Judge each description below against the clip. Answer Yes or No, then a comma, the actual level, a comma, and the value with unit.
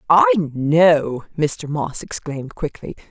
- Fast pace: No, slow, 115 wpm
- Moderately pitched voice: Yes, medium, 145 Hz